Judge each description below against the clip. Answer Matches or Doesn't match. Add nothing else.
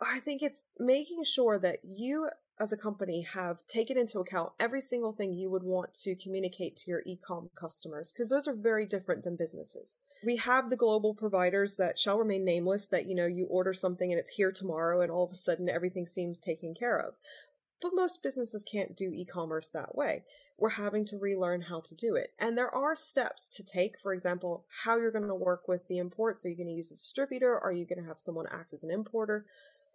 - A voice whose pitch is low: Doesn't match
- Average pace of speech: Doesn't match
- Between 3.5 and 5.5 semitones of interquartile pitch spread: Matches